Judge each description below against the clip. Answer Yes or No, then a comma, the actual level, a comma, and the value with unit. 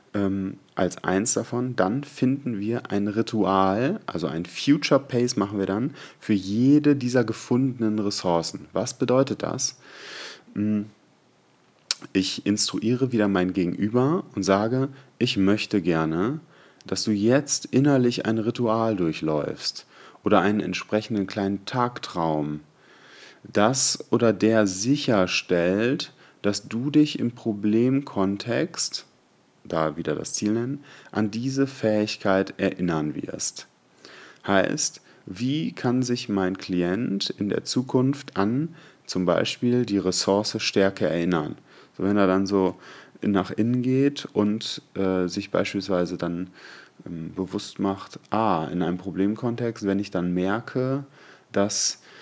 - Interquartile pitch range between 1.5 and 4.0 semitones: No, average, 4.4 semitones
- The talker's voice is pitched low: Yes, low, 105 Hz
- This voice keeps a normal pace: No, slow, 120 wpm